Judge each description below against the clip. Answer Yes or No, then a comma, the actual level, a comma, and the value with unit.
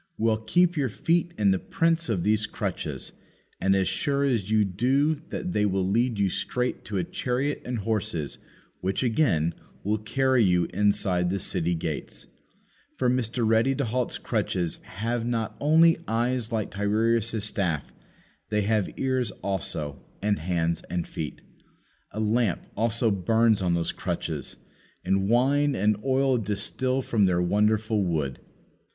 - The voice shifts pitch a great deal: No, average, 4.5 semitones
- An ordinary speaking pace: Yes, average, 150 wpm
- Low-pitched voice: Yes, low, 110 Hz